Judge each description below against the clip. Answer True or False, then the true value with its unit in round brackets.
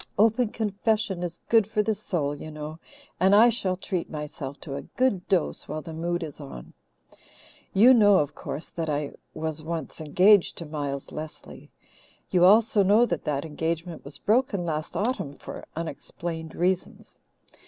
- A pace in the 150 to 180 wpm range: True (165 wpm)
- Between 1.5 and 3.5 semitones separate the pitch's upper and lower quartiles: False (4.9 semitones)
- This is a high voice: False (170 Hz)